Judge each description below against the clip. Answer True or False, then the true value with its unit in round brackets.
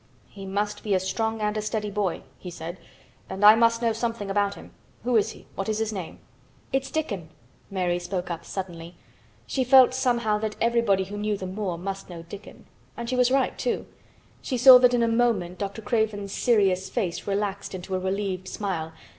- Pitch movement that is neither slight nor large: True (3.4 semitones)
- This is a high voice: True (205 Hz)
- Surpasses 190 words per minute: True (200 wpm)